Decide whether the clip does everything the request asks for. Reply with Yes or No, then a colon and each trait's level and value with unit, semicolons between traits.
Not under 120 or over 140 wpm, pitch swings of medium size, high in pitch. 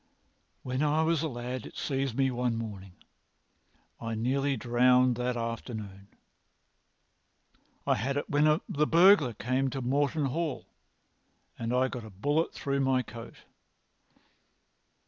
No: slow, 135 wpm; average, 3.3 semitones; low, 130 Hz